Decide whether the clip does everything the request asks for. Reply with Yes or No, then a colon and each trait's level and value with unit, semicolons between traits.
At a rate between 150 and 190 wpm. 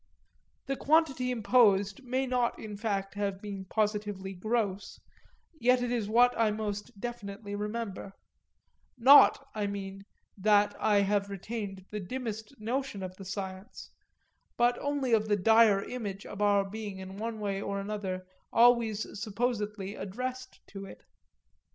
No: average, 140 wpm